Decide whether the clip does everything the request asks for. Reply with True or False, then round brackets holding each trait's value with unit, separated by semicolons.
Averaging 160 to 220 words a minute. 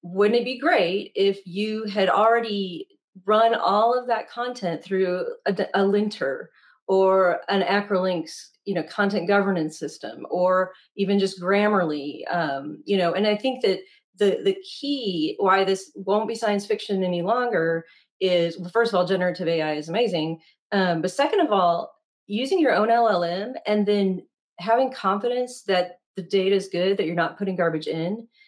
True (170 wpm)